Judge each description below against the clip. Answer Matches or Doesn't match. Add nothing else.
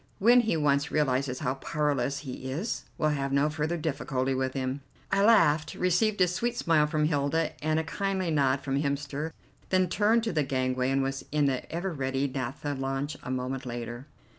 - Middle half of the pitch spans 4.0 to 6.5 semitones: Doesn't match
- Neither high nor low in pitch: Matches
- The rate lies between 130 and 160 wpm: Doesn't match